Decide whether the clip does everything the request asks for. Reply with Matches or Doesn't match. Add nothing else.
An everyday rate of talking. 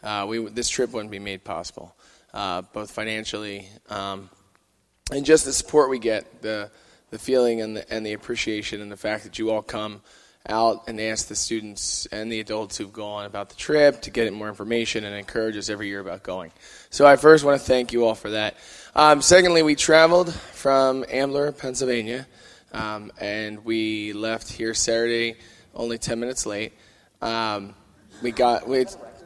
Matches